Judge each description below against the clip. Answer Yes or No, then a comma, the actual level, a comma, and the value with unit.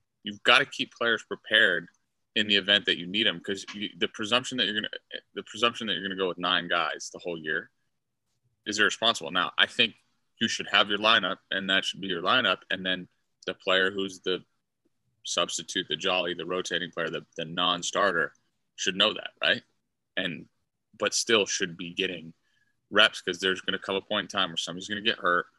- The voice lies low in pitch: Yes, very low, 95 Hz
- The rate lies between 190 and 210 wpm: Yes, average, 200 wpm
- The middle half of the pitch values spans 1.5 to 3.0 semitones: Yes, narrow, 2.5 semitones